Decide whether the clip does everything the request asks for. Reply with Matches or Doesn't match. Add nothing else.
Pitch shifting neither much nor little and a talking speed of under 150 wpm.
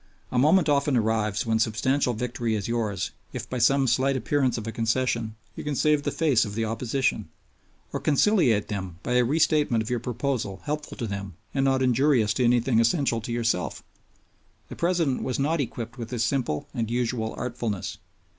Doesn't match